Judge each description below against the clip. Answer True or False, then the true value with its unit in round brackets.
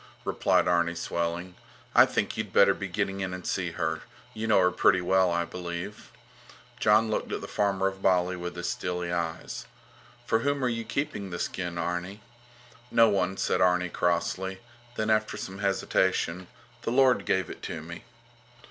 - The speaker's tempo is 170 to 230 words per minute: True (175 wpm)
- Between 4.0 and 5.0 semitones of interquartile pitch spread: False (2.7 semitones)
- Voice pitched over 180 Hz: False (95 Hz)